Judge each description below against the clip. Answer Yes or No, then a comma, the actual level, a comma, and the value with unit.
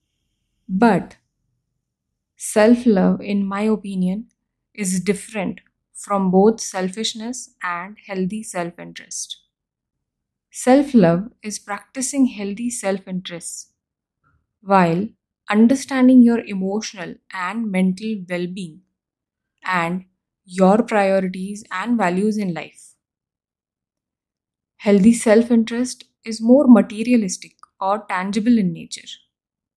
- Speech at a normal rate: No, slow, 95 wpm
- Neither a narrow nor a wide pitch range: Yes, average, 3.5 semitones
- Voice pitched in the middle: No, high, 205 Hz